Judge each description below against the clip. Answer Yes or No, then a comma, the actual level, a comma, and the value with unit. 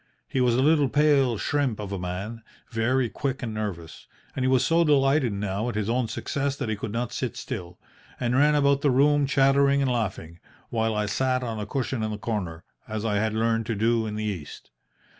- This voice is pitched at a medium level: No, low, 115 Hz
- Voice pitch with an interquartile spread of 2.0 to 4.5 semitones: Yes, average, 4.2 semitones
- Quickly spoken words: Yes, fast, 215 wpm